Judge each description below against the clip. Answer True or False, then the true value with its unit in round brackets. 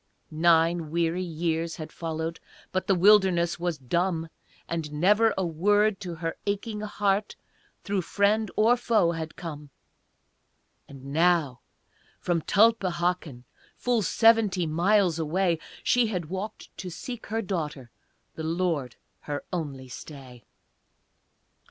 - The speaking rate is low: True (120 wpm)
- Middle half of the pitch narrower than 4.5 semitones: True (4.0 semitones)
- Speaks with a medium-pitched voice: True (175 Hz)